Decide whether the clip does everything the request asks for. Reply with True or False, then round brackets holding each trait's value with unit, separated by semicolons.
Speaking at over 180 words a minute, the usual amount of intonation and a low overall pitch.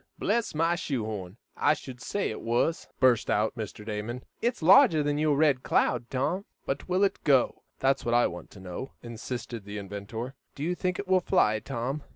False (200 wpm; 6.2 semitones; 130 Hz)